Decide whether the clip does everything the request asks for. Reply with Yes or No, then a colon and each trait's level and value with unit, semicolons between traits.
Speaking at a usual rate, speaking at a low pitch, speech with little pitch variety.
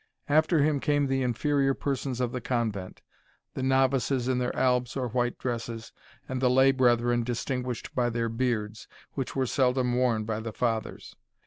Yes: average, 170 wpm; low, 125 Hz; narrow, 2.1 semitones